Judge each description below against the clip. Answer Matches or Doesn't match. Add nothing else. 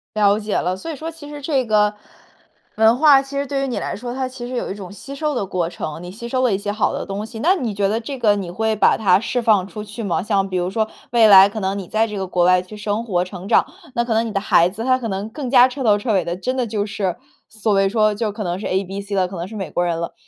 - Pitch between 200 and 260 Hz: Matches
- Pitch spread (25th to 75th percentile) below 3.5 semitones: Doesn't match